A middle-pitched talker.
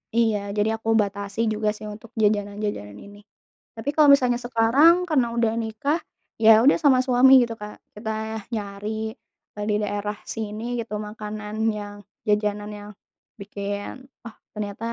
No: high, 210 Hz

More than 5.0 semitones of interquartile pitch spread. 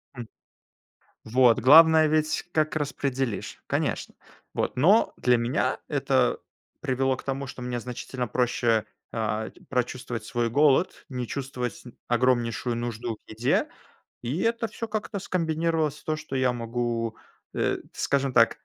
No: average, 4.2 semitones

